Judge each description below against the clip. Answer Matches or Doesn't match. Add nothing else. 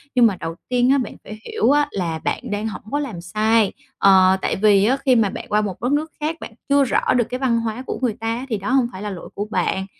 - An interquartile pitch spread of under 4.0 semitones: Doesn't match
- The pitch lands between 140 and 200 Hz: Doesn't match